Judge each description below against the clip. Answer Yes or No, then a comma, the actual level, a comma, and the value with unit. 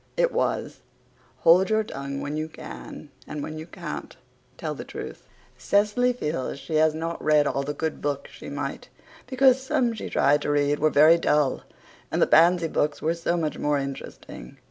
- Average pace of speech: Yes, average, 185 wpm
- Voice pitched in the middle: Yes, medium, 155 Hz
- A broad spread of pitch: No, average, 3.6 semitones